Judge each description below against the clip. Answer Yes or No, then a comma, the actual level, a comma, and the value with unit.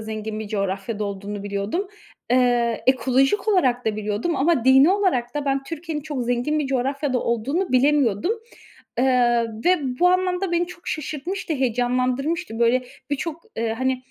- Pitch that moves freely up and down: No, average, 4.8 semitones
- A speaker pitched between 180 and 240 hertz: No, very high, 260 Hz